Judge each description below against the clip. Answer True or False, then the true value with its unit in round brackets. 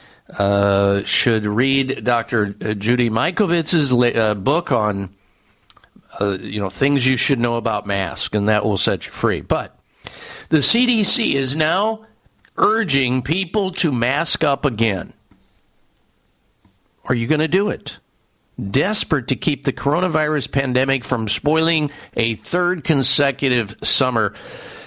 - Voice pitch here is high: False (135 Hz)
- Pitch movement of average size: False (6.2 semitones)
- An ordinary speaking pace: False (130 wpm)